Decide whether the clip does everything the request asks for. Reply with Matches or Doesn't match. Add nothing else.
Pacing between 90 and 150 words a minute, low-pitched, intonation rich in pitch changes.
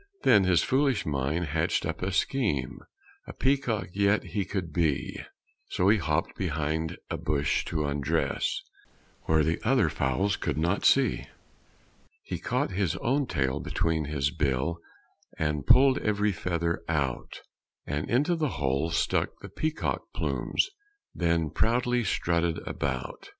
Matches